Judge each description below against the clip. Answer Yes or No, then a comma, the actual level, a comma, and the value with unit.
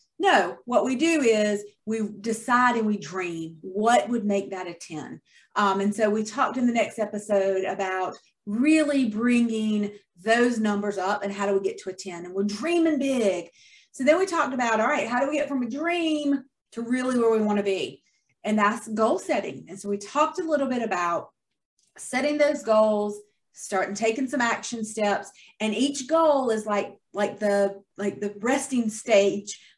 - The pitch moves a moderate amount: Yes, average, 4.1 semitones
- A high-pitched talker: Yes, high, 215 Hz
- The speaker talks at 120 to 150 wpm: No, average, 190 wpm